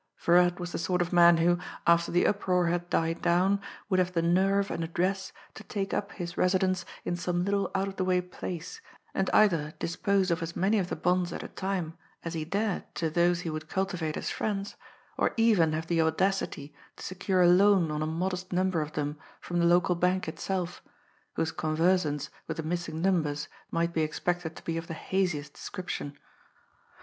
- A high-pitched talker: No, medium, 175 Hz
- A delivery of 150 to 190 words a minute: No, average, 200 wpm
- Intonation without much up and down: Yes, narrow, 2.3 semitones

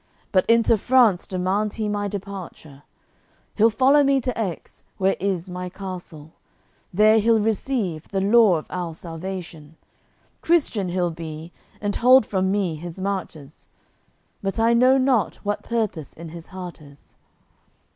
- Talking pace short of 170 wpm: Yes, average, 145 wpm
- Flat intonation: No, average, 4.4 semitones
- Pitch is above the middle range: Yes, high, 195 Hz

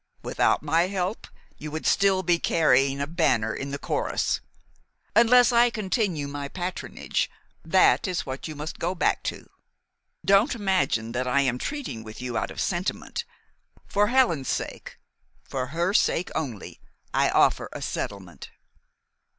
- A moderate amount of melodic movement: No, wide, 6.6 semitones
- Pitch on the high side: No, medium, 165 Hz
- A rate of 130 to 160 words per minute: Yes, average, 150 wpm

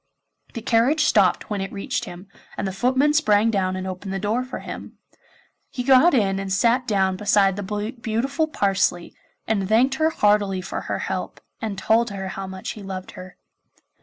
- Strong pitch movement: No, average, 3.7 semitones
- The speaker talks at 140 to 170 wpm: No, average, 185 wpm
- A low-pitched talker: No, high, 205 Hz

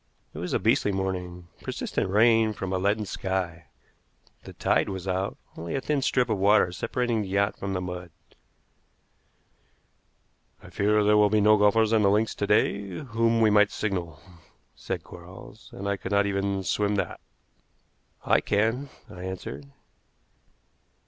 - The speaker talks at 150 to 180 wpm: Yes, average, 160 wpm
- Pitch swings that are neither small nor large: No, narrow, 2.3 semitones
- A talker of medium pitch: No, low, 100 Hz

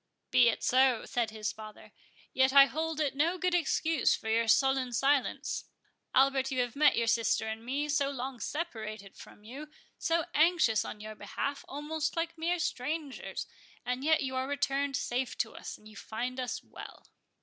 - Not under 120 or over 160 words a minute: No, average, 180 wpm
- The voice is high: Yes, very high, 265 Hz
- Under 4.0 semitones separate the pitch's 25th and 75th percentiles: No, average, 4.4 semitones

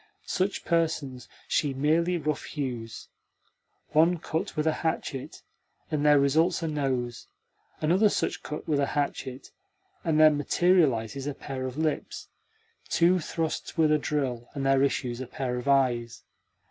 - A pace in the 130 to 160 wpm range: Yes, average, 145 wpm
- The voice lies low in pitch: No, medium, 145 Hz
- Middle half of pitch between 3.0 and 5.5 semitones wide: Yes, average, 3.4 semitones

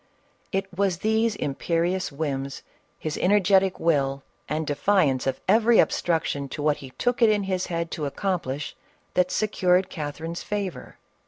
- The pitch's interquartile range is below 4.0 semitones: No, average, 4.9 semitones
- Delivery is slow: No, average, 145 wpm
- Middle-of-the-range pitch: Yes, medium, 175 Hz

